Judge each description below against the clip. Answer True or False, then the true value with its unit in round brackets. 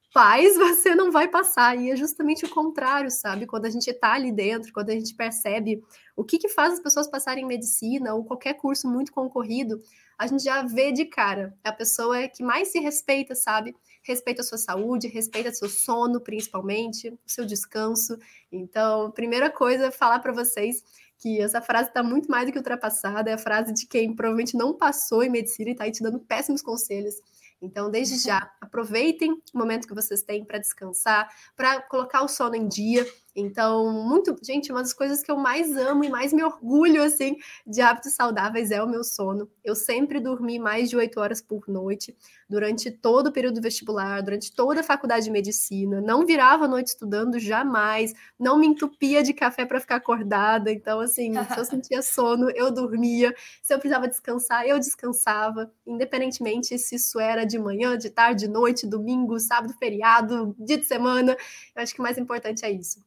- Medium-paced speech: False (195 wpm)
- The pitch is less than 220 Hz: False (240 Hz)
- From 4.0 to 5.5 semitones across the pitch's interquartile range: False (3.1 semitones)